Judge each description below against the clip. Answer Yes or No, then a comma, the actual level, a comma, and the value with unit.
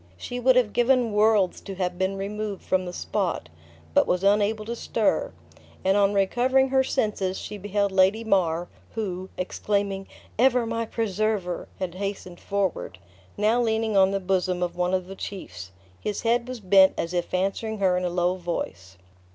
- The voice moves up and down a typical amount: Yes, average, 3.1 semitones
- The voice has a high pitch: Yes, high, 195 Hz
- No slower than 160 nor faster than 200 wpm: Yes, average, 175 wpm